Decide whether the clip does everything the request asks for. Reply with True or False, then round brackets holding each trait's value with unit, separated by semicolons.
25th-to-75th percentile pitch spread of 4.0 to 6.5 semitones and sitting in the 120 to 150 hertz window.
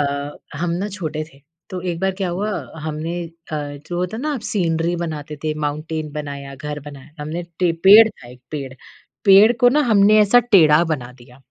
False (4.8 semitones; 160 Hz)